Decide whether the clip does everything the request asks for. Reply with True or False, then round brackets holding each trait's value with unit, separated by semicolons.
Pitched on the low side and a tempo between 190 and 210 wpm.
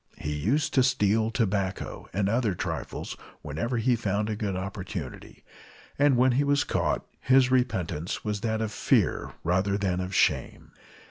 False (105 Hz; 155 wpm)